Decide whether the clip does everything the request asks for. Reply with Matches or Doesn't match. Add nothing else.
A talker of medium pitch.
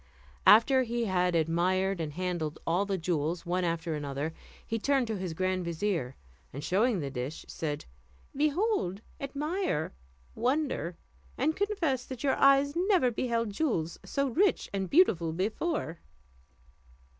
Doesn't match